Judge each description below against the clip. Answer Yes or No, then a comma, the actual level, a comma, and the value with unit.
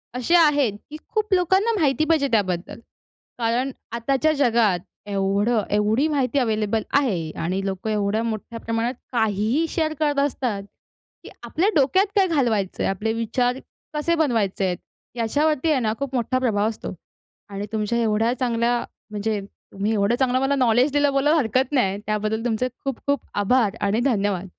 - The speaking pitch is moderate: No, high, 235 Hz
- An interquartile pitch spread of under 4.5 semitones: No, average, 4.8 semitones